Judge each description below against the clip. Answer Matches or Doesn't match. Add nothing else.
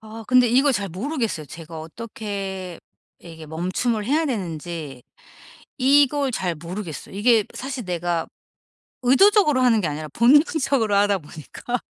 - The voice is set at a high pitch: Matches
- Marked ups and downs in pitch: Matches